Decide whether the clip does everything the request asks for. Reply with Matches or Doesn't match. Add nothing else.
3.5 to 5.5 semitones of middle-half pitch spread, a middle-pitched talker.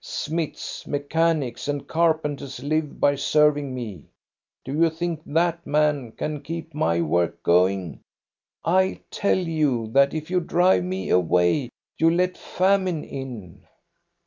Matches